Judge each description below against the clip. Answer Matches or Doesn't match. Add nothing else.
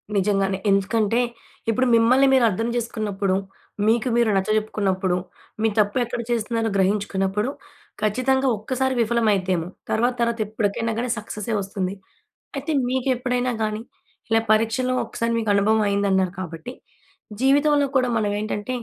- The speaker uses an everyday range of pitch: Matches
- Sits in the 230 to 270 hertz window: Doesn't match